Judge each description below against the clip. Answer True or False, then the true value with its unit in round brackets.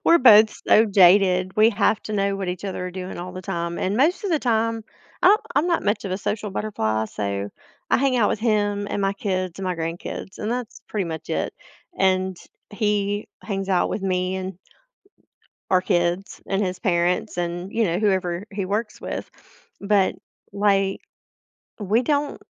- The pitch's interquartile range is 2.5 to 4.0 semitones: True (2.8 semitones)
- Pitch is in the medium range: False (195 Hz)